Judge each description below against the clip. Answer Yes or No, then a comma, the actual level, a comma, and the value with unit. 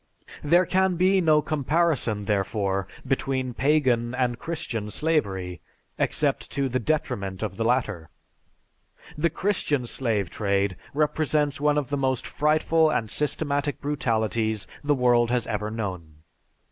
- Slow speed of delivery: Yes, slow, 130 wpm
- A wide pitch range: Yes, wide, 5.8 semitones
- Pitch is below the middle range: Yes, low, 130 Hz